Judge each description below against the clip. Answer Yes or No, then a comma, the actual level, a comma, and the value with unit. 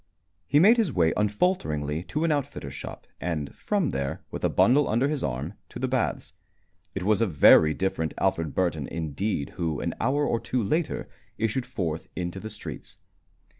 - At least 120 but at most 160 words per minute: No, average, 175 wpm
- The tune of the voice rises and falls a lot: Yes, wide, 8.7 semitones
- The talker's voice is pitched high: No, very low, 95 Hz